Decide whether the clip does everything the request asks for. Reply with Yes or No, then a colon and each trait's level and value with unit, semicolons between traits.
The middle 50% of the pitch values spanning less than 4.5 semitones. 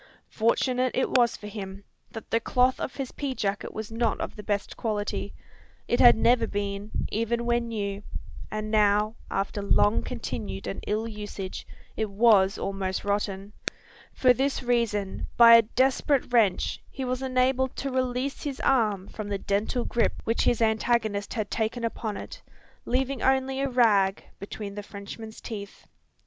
Yes: average, 3.4 semitones